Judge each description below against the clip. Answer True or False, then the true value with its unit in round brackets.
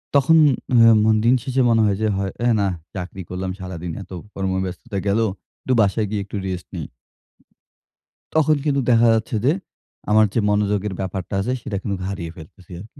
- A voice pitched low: True (105 Hz)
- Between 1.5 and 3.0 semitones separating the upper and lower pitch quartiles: False (3.6 semitones)